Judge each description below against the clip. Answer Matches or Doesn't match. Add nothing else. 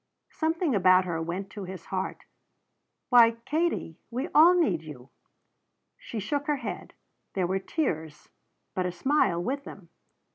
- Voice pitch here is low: Doesn't match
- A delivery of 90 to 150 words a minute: Matches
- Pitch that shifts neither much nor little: Doesn't match